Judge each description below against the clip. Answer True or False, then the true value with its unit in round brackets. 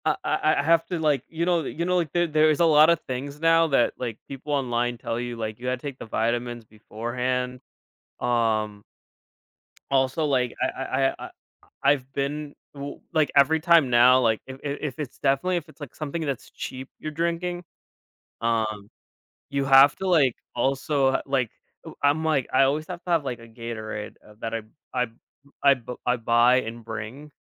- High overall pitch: False (135 Hz)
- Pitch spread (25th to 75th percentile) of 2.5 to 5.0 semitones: True (4.2 semitones)